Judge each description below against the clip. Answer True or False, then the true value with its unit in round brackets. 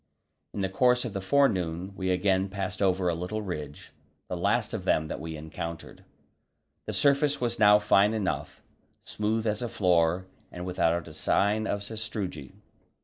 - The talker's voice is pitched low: True (95 Hz)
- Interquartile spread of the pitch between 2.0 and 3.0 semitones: False (3.4 semitones)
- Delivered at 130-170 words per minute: True (165 wpm)